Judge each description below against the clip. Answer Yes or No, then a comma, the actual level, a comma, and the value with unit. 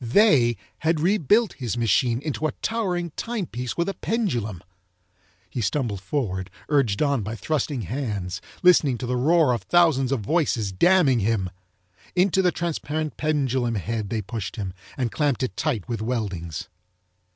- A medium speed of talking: Yes, average, 150 wpm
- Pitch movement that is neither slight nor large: No, wide, 6.4 semitones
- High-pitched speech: No, low, 130 Hz